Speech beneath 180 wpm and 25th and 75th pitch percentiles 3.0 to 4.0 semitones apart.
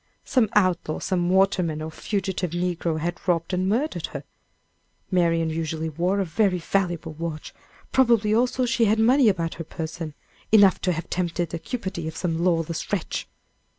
Yes: average, 160 wpm; average, 3.4 semitones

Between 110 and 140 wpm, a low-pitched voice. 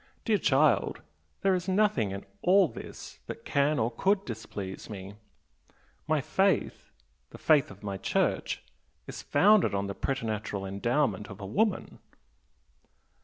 Yes: slow, 135 wpm; low, 130 Hz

